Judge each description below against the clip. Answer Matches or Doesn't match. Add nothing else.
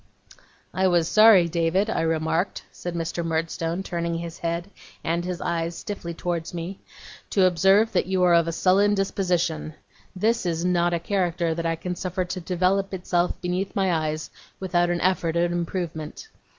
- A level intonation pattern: Matches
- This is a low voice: Doesn't match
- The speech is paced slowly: Doesn't match